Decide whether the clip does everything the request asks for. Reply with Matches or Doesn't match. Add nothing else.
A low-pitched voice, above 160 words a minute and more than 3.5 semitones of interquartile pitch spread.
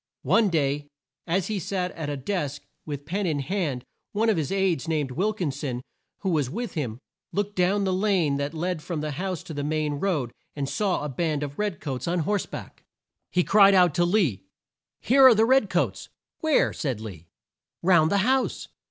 Doesn't match